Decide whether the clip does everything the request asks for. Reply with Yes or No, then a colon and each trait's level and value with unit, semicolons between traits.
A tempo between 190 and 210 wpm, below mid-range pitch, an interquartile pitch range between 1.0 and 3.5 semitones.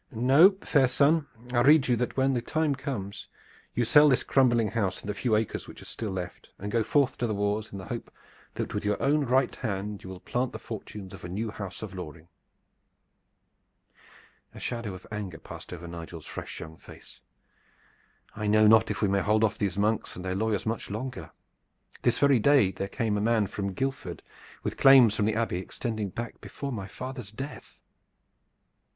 No: average, 200 wpm; low, 110 Hz; average, 4.4 semitones